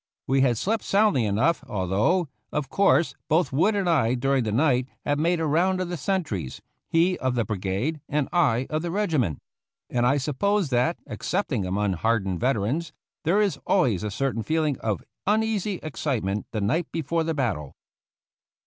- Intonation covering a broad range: Yes, wide, 7.3 semitones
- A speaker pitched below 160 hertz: Yes, medium, 140 Hz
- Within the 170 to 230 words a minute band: Yes, average, 175 wpm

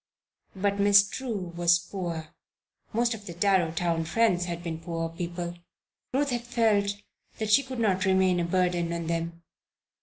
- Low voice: No, medium, 180 Hz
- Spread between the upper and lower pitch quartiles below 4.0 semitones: Yes, average, 3.3 semitones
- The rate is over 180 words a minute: No, average, 155 wpm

